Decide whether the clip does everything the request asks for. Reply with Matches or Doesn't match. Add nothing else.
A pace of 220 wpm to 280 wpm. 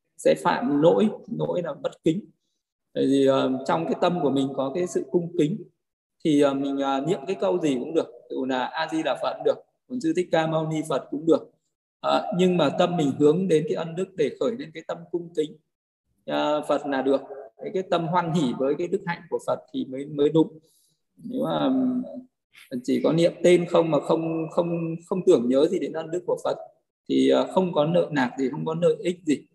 Matches